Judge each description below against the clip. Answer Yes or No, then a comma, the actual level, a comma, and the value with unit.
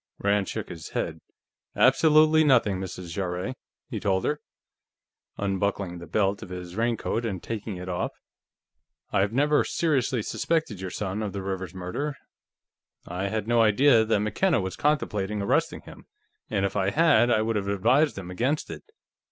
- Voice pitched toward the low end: Yes, low, 105 Hz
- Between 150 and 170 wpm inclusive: Yes, average, 165 wpm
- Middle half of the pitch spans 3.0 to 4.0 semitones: No, average, 4.8 semitones